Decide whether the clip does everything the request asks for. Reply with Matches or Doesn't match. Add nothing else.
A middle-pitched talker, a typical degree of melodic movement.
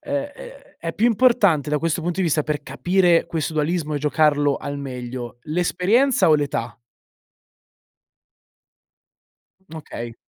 Matches